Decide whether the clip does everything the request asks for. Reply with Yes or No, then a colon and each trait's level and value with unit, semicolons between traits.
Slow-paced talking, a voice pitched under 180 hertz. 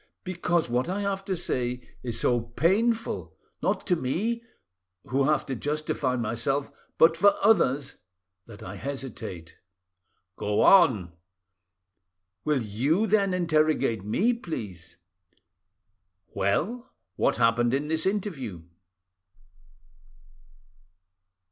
Yes: slow, 100 wpm; medium, 140 Hz